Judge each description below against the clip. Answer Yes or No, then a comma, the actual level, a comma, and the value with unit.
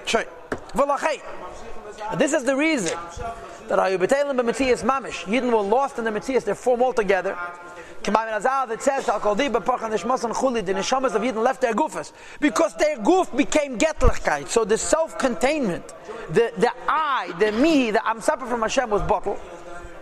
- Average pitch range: Yes, average, 4.1 semitones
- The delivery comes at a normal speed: Yes, average, 185 wpm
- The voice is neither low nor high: No, high, 235 Hz